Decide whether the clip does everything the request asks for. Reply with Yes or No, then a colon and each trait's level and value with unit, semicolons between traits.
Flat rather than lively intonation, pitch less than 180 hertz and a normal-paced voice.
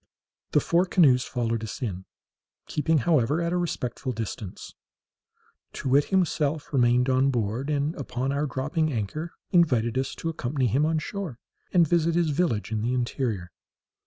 No: average, 4.8 semitones; low, 135 Hz; average, 160 wpm